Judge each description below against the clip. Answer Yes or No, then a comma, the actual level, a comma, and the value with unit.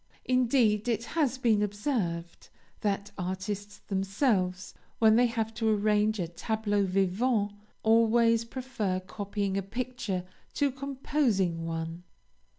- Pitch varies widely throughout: No, average, 3.6 semitones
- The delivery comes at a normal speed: No, slow, 115 wpm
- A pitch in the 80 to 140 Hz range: No, high, 210 Hz